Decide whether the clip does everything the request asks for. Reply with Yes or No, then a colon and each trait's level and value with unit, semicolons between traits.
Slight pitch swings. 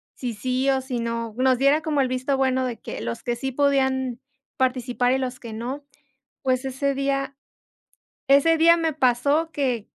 Yes: narrow, 1.9 semitones